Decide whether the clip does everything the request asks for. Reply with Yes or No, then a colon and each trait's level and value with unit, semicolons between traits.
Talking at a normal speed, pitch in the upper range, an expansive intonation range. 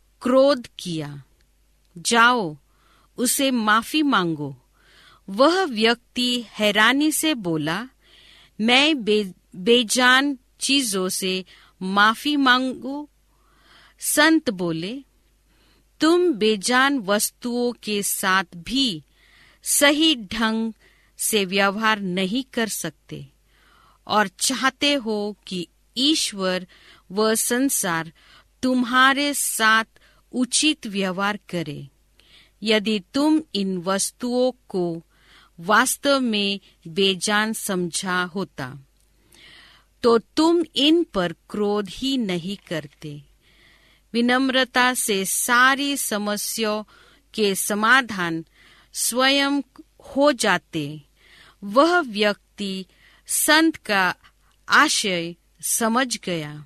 No: slow, 85 wpm; high, 220 Hz; wide, 5.7 semitones